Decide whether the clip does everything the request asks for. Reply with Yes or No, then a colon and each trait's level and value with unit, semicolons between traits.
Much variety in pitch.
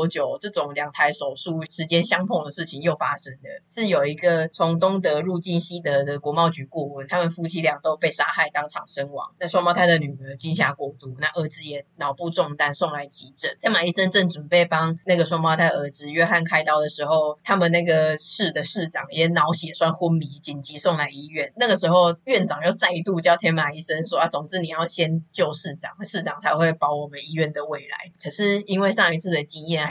No: average, 2.9 semitones